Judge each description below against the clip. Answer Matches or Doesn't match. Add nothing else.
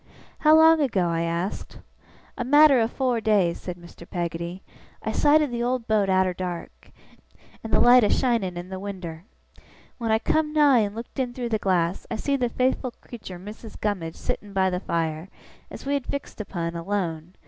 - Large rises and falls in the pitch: Matches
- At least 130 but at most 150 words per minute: Doesn't match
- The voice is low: Doesn't match